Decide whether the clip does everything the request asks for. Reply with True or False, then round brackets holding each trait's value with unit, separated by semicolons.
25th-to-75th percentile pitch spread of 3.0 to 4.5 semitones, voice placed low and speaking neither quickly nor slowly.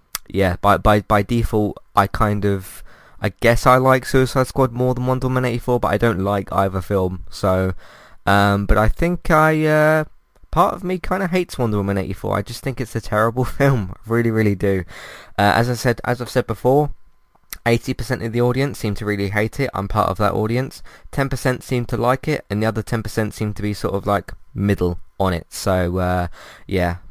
False (4.2 semitones; 110 Hz; 210 wpm)